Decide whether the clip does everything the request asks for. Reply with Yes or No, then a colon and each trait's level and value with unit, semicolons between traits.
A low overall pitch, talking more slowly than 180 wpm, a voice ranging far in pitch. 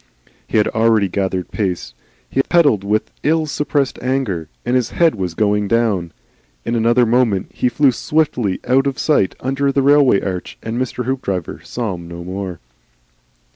Yes: low, 115 Hz; average, 165 wpm; wide, 5.7 semitones